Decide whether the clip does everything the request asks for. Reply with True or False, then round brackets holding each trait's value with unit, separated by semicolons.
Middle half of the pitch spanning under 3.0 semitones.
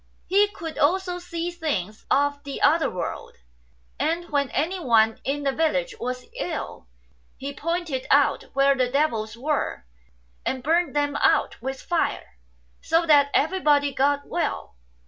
False (3.9 semitones)